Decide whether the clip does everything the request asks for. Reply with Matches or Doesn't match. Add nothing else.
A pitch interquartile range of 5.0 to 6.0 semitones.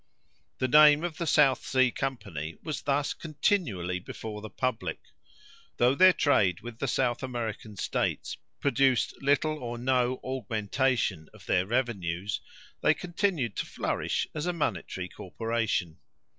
Matches